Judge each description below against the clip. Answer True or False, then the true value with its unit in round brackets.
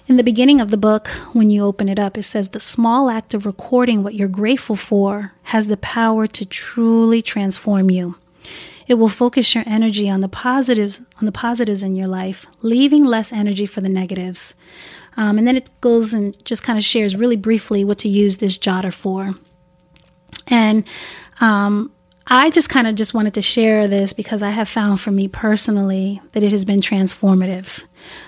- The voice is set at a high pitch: True (210 Hz)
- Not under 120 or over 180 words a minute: False (190 wpm)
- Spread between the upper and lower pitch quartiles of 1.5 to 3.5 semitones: True (2.5 semitones)